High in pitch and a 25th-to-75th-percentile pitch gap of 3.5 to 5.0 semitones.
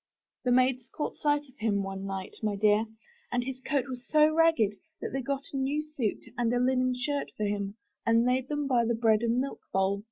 Yes: high, 245 Hz; average, 4.0 semitones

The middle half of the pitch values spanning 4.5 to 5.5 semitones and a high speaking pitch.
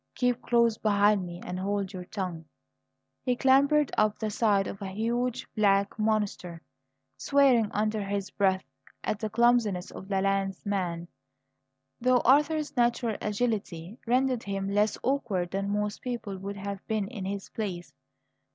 No: average, 3.4 semitones; high, 205 Hz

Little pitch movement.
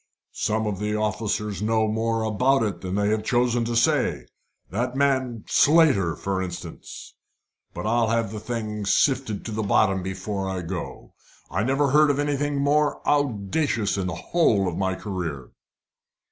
No: average, 4.8 semitones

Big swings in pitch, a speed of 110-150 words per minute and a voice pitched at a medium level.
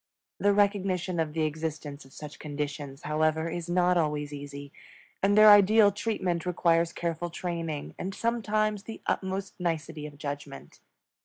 No: average, 4.5 semitones; average, 145 wpm; medium, 165 Hz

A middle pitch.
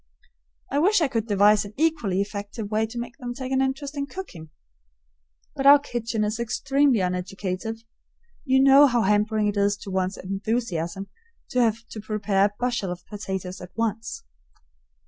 No: high, 220 Hz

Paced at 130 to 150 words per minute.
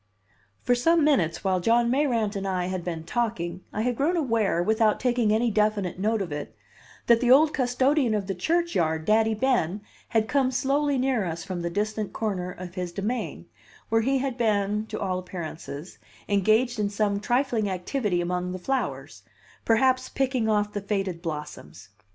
No: average, 175 wpm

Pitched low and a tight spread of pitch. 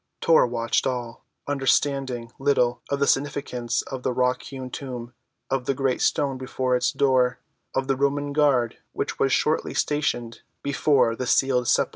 Yes: low, 130 Hz; narrow, 2.2 semitones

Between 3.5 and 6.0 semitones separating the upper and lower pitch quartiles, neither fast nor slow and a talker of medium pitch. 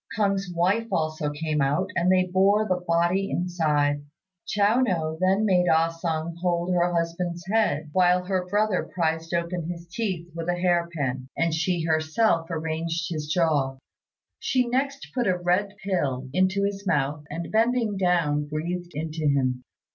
No: average, 3.0 semitones; average, 160 wpm; medium, 175 Hz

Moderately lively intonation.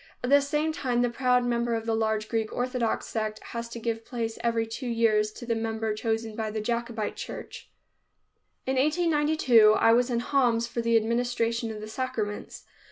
No: narrow, 1.8 semitones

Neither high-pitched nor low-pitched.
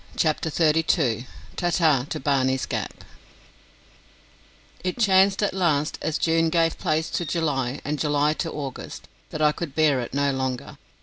Yes: medium, 155 Hz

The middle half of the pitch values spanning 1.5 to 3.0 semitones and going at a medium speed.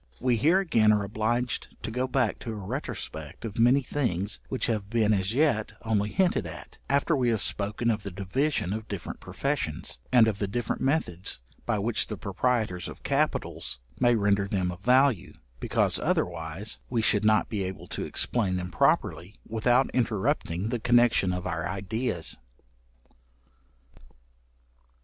No: average, 4.0 semitones; average, 160 wpm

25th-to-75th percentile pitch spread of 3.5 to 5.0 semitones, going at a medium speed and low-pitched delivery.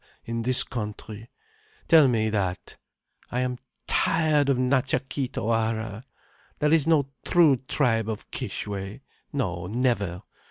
No: average, 4.4 semitones; slow, 115 wpm; low, 125 Hz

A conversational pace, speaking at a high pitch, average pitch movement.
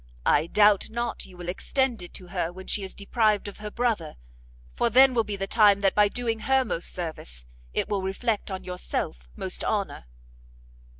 Yes: average, 190 wpm; high, 200 Hz; average, 3.8 semitones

